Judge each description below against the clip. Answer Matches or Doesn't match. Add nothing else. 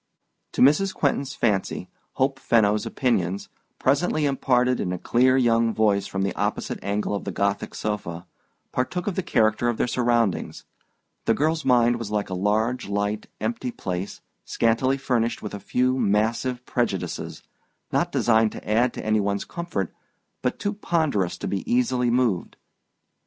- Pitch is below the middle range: Matches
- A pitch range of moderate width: Matches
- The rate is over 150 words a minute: Matches